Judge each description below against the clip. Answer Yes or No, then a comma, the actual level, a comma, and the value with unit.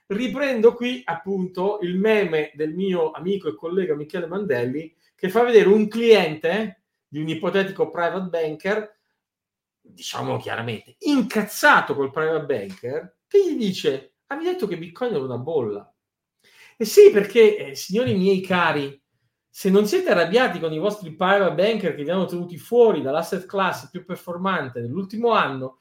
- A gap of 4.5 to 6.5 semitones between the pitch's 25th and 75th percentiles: Yes, average, 4.9 semitones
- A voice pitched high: Yes, high, 195 Hz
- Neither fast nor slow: Yes, average, 150 wpm